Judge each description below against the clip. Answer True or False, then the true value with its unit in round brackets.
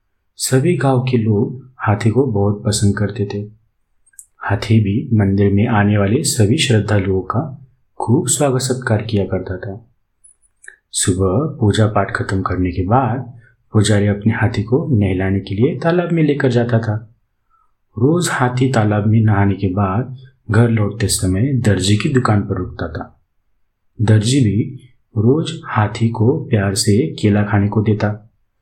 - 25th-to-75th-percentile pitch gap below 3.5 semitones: False (3.8 semitones)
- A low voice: True (110 Hz)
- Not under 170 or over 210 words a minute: False (150 wpm)